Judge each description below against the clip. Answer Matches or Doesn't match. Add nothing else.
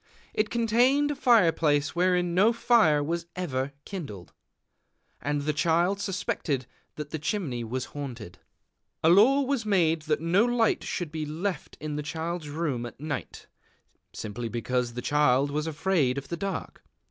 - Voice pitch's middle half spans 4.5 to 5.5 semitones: Matches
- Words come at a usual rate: Matches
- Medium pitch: Matches